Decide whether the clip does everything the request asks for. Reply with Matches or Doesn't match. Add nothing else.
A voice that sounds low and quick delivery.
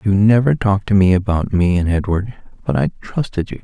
Matches